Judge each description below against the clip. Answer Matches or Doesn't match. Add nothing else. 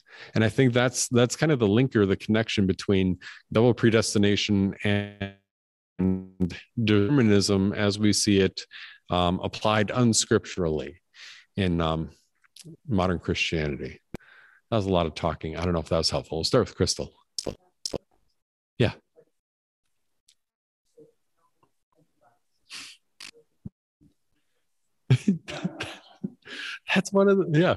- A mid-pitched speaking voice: Doesn't match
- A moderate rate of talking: Doesn't match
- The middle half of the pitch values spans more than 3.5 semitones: Matches